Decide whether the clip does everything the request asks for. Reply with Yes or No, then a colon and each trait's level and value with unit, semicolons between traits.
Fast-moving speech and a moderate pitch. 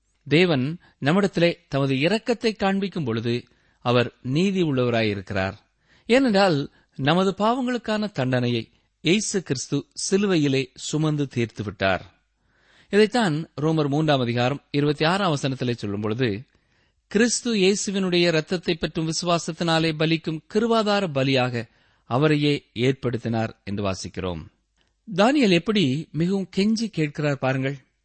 No: average, 90 wpm; medium, 150 Hz